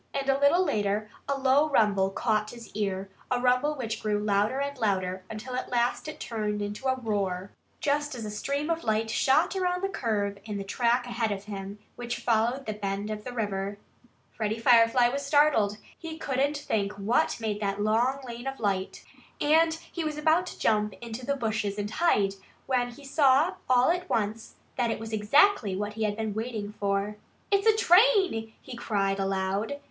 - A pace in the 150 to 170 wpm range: No, average, 190 wpm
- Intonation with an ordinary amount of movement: Yes, average, 5.0 semitones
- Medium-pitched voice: No, high, 225 Hz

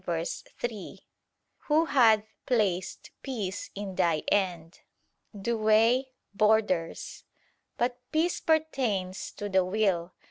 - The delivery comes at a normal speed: No, slow, 95 wpm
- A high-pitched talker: Yes, high, 210 Hz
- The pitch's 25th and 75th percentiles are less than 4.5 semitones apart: No, average, 4.8 semitones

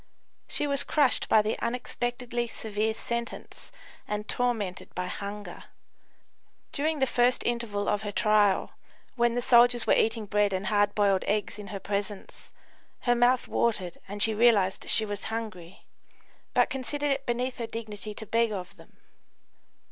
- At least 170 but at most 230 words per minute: No, average, 155 wpm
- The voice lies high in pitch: Yes, high, 220 Hz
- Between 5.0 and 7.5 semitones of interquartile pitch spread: No, average, 2.8 semitones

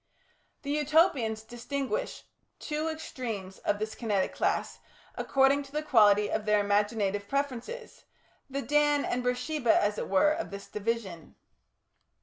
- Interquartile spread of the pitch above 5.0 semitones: Yes, wide, 5.6 semitones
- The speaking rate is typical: No, slow, 130 wpm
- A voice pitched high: Yes, high, 240 Hz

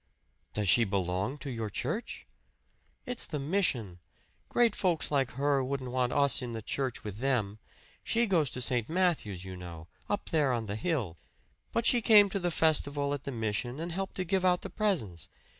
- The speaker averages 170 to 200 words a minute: Yes, average, 190 wpm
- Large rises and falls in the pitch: Yes, wide, 8.1 semitones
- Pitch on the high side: No, low, 135 Hz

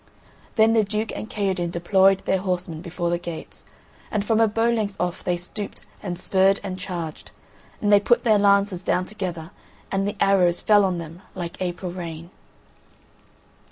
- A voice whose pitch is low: No, high, 190 Hz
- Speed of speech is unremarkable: Yes, average, 170 wpm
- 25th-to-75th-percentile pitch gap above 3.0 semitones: No, average, 2.7 semitones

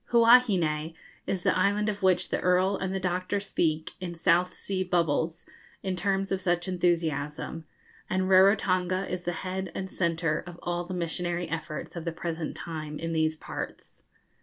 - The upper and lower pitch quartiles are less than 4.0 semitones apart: Yes, narrow, 2.4 semitones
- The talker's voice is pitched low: No, medium, 175 Hz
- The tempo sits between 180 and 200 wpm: No, average, 165 wpm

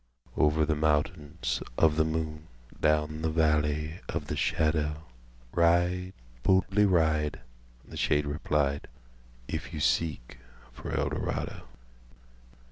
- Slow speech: Yes, slow, 90 wpm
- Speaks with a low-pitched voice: Yes, very low, 75 Hz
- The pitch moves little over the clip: Yes, narrow, 1.6 semitones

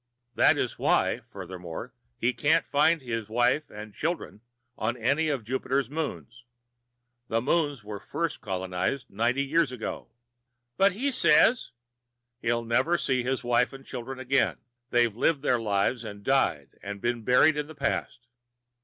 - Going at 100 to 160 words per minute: Yes, average, 155 wpm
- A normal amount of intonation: Yes, average, 3.8 semitones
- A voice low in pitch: Yes, low, 125 Hz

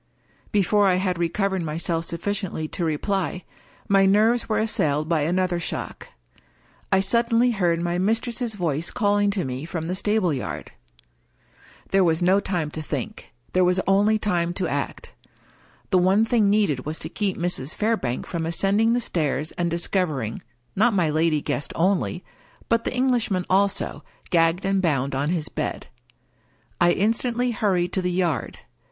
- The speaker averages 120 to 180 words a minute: Yes, average, 165 wpm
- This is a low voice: No, medium, 185 Hz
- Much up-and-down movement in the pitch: No, average, 3.8 semitones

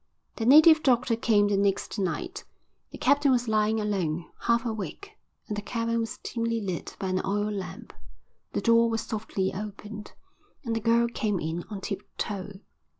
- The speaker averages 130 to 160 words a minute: No, average, 170 wpm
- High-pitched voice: Yes, high, 215 Hz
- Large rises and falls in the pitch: No, average, 2.7 semitones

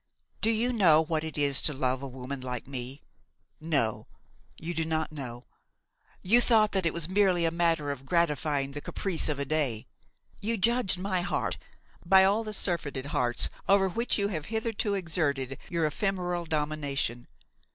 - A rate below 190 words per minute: Yes, average, 170 wpm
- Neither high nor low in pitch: Yes, medium, 160 Hz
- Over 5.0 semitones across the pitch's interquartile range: Yes, wide, 5.4 semitones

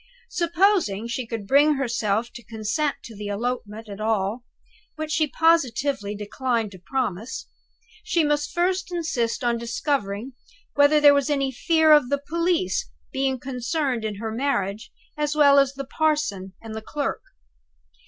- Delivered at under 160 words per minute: Yes, average, 150 wpm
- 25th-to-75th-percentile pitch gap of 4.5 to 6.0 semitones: Yes, average, 5.3 semitones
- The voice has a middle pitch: No, very high, 265 Hz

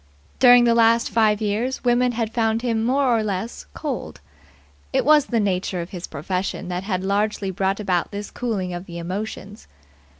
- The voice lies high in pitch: Yes, high, 210 Hz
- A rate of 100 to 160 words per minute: No, average, 175 wpm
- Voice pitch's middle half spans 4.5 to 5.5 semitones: No, average, 3.7 semitones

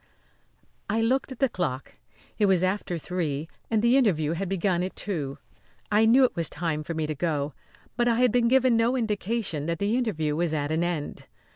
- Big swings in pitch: Yes, wide, 6.4 semitones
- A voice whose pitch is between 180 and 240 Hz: Yes, medium, 185 Hz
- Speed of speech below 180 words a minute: No, fast, 205 wpm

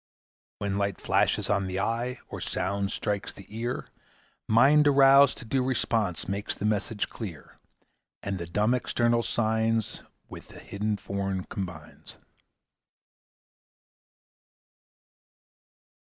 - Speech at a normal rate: No, slow, 110 wpm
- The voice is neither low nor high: No, low, 105 Hz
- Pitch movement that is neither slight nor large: Yes, average, 3.2 semitones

